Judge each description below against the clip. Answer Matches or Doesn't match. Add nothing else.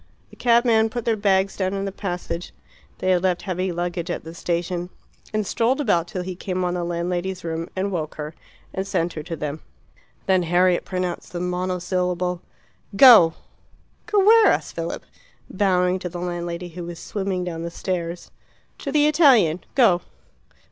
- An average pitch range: Doesn't match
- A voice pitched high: Doesn't match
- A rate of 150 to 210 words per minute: Matches